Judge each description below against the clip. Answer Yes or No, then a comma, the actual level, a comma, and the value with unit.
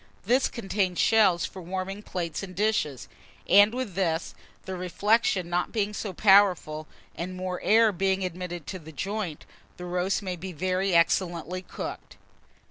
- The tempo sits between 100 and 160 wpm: Yes, average, 150 wpm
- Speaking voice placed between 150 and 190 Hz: Yes, medium, 185 Hz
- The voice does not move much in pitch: Yes, narrow, 2.3 semitones